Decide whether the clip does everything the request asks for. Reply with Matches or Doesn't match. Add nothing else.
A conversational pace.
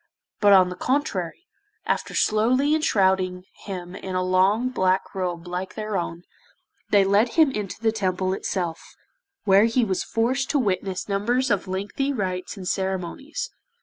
Matches